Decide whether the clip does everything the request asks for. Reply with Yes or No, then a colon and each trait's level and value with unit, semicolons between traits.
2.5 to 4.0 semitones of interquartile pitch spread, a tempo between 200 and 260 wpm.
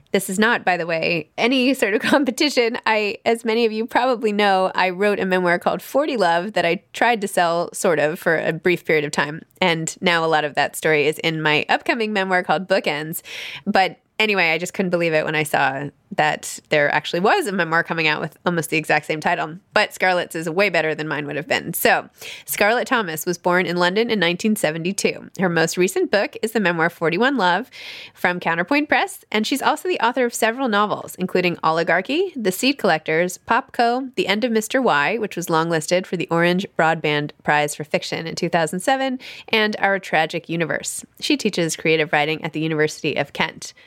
No: average, 5.2 semitones; fast, 205 wpm